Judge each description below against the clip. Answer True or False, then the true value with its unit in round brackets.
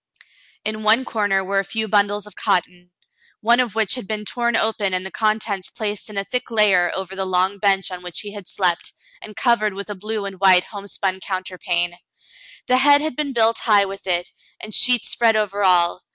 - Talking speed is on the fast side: True (210 wpm)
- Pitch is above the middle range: True (205 Hz)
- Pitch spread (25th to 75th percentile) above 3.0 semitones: False (2.7 semitones)